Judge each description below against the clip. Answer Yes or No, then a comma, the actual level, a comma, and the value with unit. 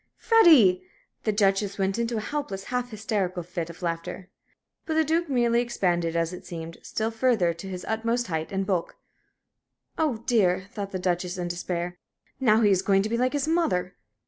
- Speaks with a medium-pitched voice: No, high, 195 Hz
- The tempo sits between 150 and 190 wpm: Yes, average, 185 wpm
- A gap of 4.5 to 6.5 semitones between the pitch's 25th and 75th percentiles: Yes, average, 4.9 semitones